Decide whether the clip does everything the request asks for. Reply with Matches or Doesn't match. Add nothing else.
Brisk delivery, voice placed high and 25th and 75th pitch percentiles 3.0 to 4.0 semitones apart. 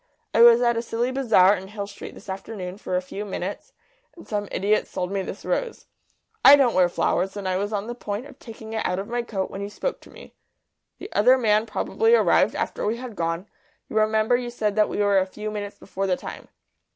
Matches